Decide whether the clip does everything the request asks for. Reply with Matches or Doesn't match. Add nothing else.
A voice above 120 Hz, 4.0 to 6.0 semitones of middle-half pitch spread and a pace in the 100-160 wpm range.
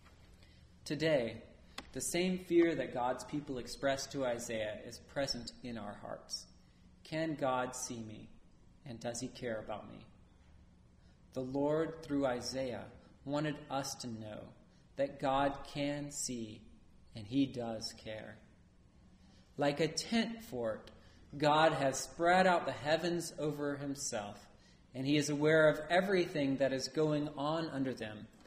Matches